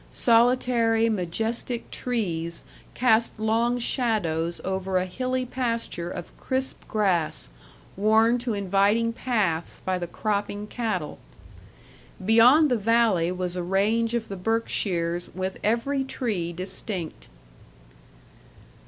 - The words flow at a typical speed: No, slow, 110 wpm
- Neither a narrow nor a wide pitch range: Yes, average, 4.3 semitones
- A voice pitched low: No, high, 215 Hz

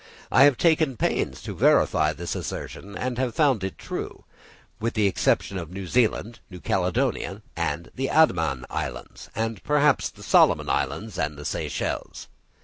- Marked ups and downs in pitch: Yes, wide, 6.8 semitones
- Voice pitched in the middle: No, low, 100 Hz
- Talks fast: No, average, 150 wpm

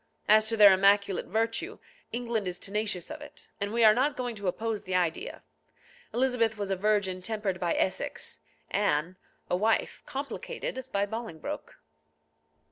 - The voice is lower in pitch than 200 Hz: No, high, 210 Hz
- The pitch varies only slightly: No, average, 3.2 semitones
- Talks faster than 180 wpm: No, average, 150 wpm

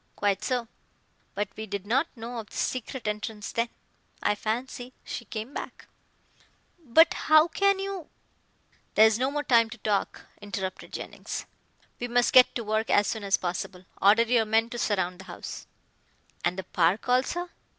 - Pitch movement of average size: Yes, average, 3.6 semitones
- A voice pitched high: Yes, high, 225 Hz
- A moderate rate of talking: Yes, average, 170 wpm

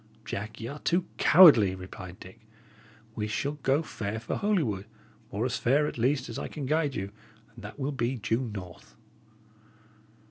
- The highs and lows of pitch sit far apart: Yes, wide, 5.8 semitones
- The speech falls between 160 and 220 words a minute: Yes, average, 170 wpm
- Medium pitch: No, low, 120 Hz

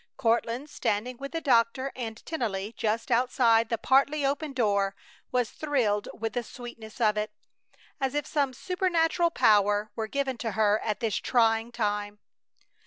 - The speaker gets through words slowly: No, average, 155 wpm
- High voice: Yes, high, 235 Hz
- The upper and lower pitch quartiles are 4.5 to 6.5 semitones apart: No, average, 4.0 semitones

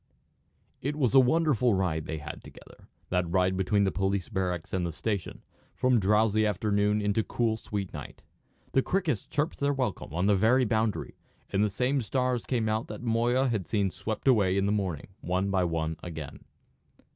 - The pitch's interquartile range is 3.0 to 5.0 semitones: Yes, average, 4.6 semitones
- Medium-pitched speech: No, low, 105 Hz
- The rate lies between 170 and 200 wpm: Yes, average, 185 wpm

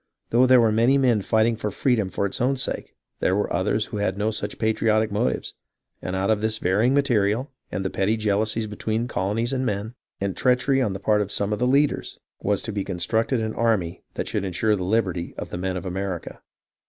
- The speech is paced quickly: Yes, fast, 215 wpm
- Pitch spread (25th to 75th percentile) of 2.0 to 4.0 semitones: Yes, average, 2.9 semitones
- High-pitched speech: No, low, 110 Hz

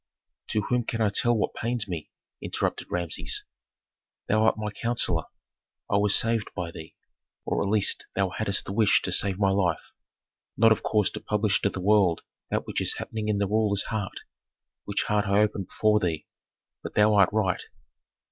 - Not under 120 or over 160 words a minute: No, average, 185 wpm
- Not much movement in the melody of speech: Yes, narrow, 1.9 semitones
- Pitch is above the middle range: No, low, 105 Hz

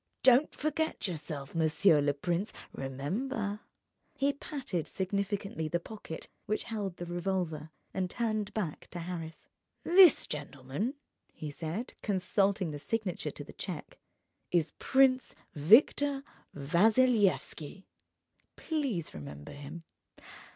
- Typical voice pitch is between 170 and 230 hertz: Yes, medium, 185 Hz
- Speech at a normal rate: No, slow, 115 wpm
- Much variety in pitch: Yes, wide, 6.2 semitones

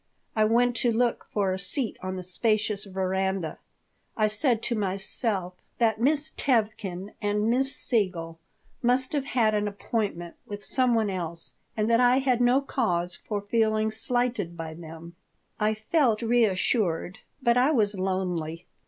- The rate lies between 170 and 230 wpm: No, average, 155 wpm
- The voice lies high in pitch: Yes, high, 215 Hz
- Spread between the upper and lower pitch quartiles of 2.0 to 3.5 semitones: No, average, 4.3 semitones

